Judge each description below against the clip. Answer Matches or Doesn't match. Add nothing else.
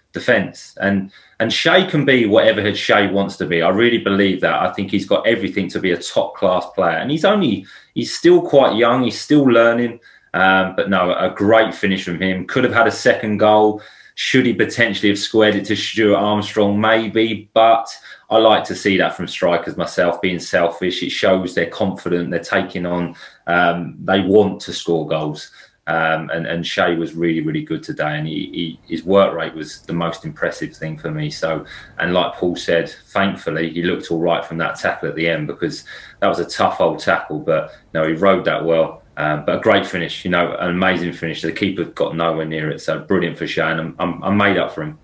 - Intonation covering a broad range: Doesn't match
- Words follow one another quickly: Matches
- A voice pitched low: Matches